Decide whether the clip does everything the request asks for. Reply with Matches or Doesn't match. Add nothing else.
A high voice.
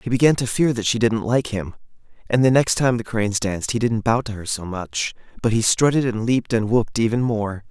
Doesn't match